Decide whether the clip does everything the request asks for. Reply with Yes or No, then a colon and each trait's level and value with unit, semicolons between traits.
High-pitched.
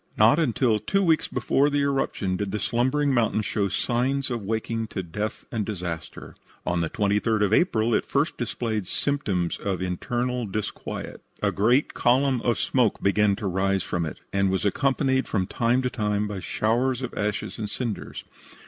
No: low, 110 Hz